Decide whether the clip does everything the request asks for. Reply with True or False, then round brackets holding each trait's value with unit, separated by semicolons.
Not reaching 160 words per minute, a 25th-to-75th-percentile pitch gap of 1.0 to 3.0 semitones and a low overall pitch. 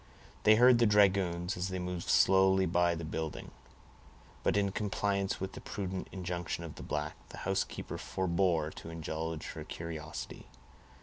True (150 wpm; 2.7 semitones; 90 Hz)